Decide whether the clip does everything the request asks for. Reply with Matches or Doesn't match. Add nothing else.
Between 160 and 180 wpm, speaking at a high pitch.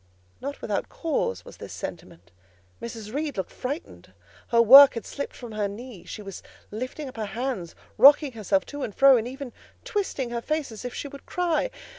Doesn't match